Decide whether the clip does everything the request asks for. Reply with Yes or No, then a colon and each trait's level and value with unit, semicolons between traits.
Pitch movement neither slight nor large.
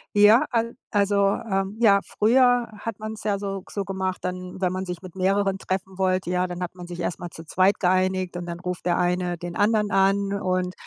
No: narrow, 2.0 semitones